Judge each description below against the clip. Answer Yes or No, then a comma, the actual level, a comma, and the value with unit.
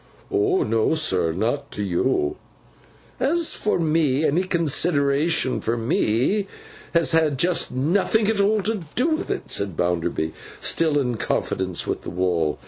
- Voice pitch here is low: No, medium, 145 Hz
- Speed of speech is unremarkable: Yes, average, 145 wpm